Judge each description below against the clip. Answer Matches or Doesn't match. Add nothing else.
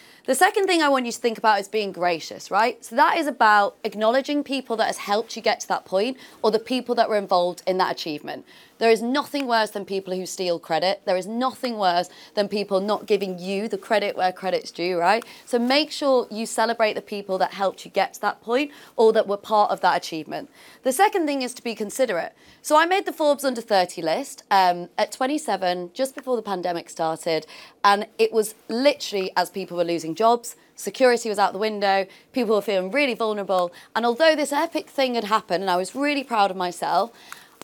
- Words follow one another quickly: Matches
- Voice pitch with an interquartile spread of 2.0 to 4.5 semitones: Doesn't match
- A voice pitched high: Matches